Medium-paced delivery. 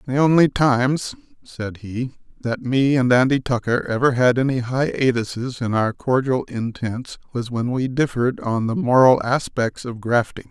Yes: average, 160 wpm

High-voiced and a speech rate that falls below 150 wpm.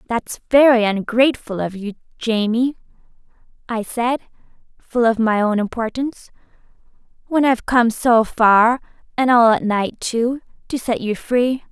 Yes: high, 235 Hz; average, 140 wpm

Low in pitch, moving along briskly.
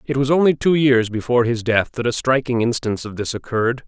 Yes: low, 125 Hz; fast, 230 wpm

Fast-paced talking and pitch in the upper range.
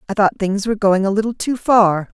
Yes: fast, 245 wpm; high, 205 Hz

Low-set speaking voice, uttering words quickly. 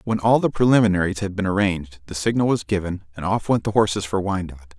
Yes: very low, 95 Hz; fast, 225 wpm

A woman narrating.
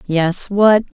Yes: female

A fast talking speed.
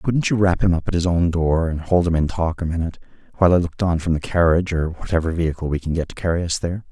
Yes: fast, 285 wpm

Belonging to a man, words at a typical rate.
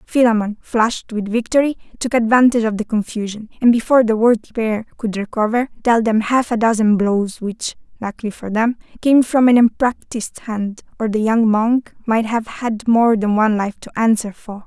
No: female; average, 185 wpm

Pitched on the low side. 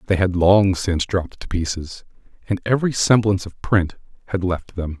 Yes: very low, 95 Hz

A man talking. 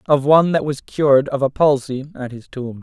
Yes: male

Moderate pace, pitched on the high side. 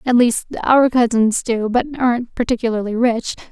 Yes: average, 155 wpm; high, 235 Hz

